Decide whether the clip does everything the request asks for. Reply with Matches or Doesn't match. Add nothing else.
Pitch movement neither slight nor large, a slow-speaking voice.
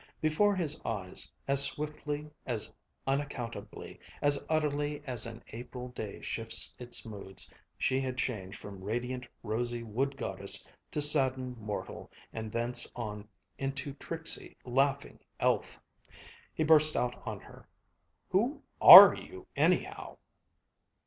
Matches